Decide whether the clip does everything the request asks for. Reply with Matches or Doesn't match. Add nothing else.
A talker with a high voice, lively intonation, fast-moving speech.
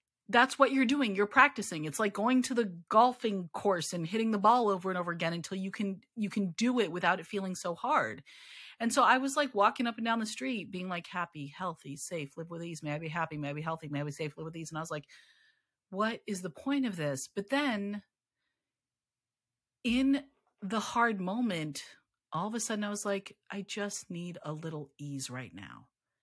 Matches